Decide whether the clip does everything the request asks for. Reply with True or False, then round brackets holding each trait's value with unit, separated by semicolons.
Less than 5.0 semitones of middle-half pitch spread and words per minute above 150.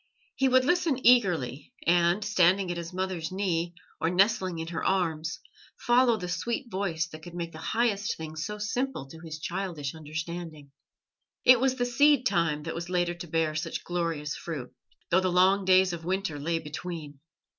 True (3.6 semitones; 175 wpm)